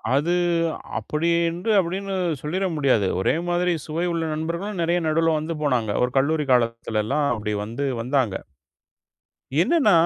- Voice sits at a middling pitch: Yes, medium, 155 Hz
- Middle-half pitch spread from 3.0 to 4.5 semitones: No, wide, 5.6 semitones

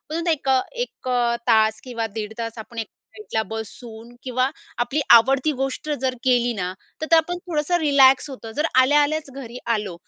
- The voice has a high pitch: Yes, very high, 255 Hz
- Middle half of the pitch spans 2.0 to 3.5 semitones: No, average, 4.4 semitones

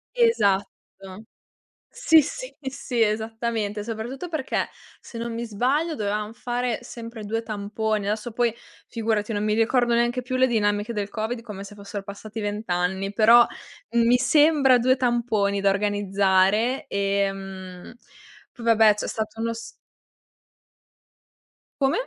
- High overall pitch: Yes, high, 220 Hz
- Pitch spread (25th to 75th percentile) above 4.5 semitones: No, average, 2.9 semitones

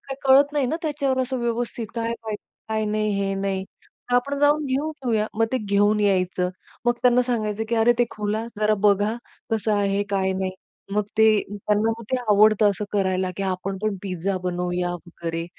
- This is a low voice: No, high, 210 Hz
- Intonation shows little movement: No, average, 3.6 semitones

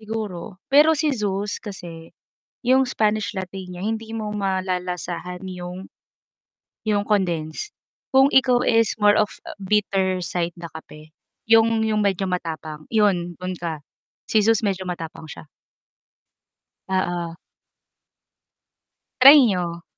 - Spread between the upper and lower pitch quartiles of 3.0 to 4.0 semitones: Yes, average, 3.7 semitones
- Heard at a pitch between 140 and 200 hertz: Yes, high, 190 Hz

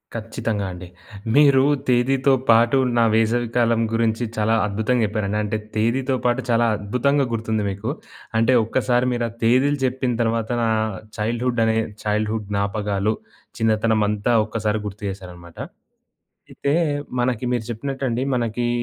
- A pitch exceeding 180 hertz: No, low, 115 Hz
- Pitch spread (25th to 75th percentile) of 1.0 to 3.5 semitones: Yes, narrow, 2.5 semitones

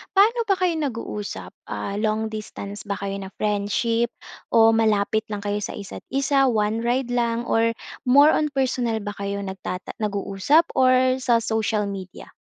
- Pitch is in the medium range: No, high, 225 Hz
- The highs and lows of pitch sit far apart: No, average, 3.8 semitones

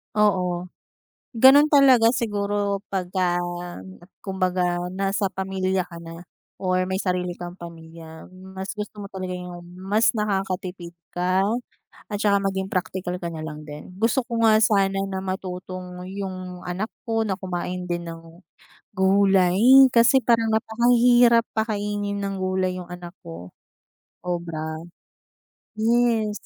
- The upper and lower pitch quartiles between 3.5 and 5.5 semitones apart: No, narrow, 2.6 semitones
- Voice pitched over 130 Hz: Yes, high, 190 Hz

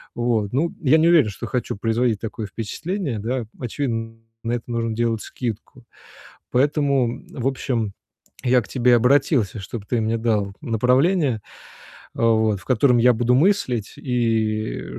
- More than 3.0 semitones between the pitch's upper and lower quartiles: No, average, 2.7 semitones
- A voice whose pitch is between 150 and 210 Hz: No, low, 120 Hz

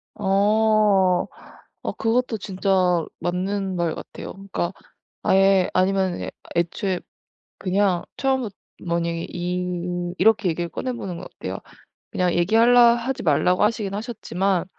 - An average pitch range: Yes, average, 3.3 semitones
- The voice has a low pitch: No, high, 190 Hz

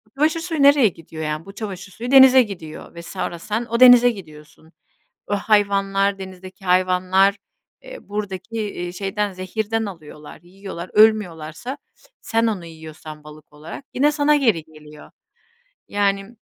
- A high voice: Yes, high, 195 Hz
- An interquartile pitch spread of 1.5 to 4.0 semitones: No, average, 4.8 semitones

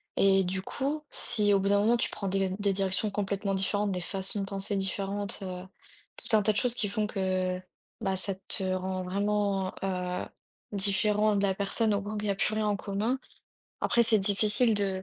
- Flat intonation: Yes, narrow, 1.5 semitones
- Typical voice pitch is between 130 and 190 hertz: No, high, 200 Hz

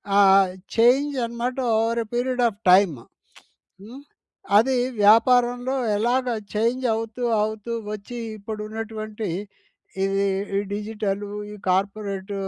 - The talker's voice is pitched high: Yes, high, 220 Hz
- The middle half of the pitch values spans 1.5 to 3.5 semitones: Yes, average, 2.9 semitones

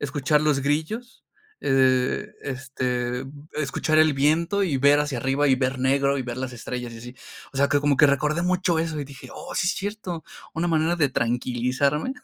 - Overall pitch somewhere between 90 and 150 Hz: Yes, medium, 140 Hz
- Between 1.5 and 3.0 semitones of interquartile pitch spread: No, average, 3.4 semitones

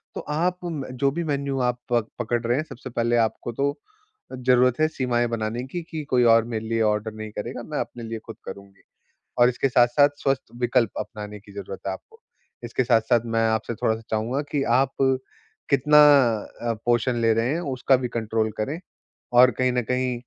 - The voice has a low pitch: Yes, low, 120 Hz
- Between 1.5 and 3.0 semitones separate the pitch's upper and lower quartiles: Yes, average, 2.7 semitones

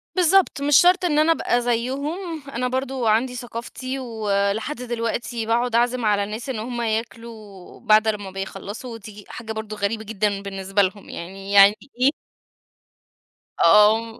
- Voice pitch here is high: Yes, high, 230 Hz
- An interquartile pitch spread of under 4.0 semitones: Yes, average, 3.4 semitones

